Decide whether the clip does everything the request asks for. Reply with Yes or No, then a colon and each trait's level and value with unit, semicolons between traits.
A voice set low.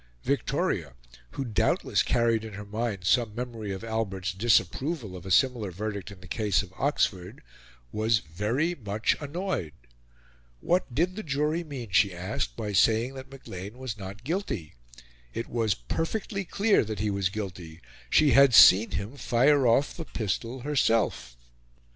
Yes: low, 110 Hz